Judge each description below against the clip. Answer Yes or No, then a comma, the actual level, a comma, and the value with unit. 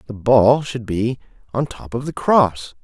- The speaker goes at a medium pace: Yes, average, 190 wpm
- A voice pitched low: Yes, low, 120 Hz